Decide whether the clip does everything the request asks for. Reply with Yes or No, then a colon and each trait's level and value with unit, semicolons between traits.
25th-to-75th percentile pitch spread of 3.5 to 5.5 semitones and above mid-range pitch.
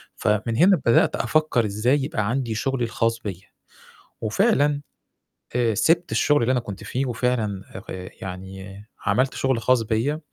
No: average, 4.2 semitones; low, 115 Hz